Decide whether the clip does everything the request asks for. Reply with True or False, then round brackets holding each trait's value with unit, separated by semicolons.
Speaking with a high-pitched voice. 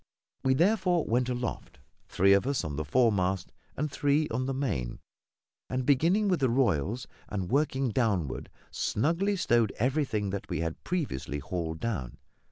False (125 Hz)